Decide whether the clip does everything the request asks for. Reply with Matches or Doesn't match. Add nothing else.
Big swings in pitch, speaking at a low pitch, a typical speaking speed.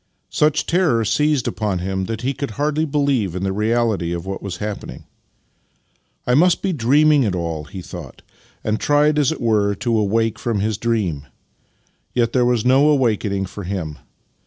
Matches